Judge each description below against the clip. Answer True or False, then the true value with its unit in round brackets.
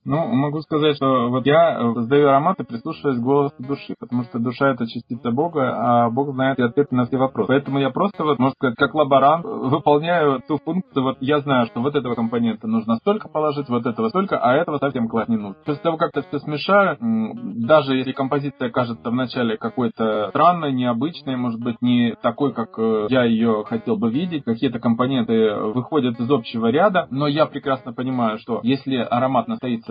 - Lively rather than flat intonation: False (3.7 semitones)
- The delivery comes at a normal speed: False (185 wpm)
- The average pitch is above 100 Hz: True (135 Hz)